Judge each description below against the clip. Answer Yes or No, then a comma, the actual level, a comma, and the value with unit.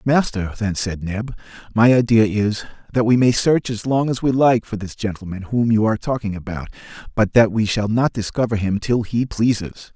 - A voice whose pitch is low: Yes, low, 110 Hz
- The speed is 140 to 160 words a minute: No, fast, 205 wpm